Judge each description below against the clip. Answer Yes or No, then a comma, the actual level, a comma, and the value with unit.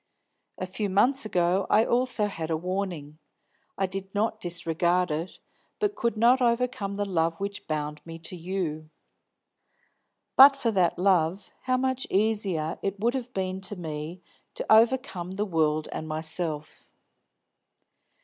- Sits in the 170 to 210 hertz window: Yes, high, 190 Hz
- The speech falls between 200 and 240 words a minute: No, average, 150 wpm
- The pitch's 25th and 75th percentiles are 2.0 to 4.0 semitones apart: No, average, 5.0 semitones